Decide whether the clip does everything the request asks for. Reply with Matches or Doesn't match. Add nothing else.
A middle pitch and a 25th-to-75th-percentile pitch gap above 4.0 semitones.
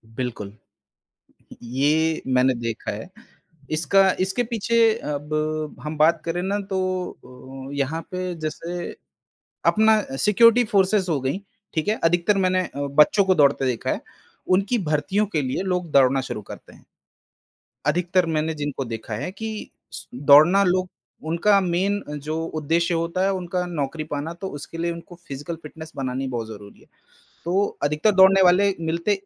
Matches